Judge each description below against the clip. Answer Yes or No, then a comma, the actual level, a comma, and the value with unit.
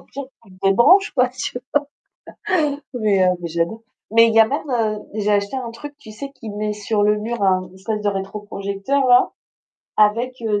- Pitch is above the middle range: Yes, high, 215 Hz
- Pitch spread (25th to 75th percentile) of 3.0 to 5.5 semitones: Yes, average, 3.4 semitones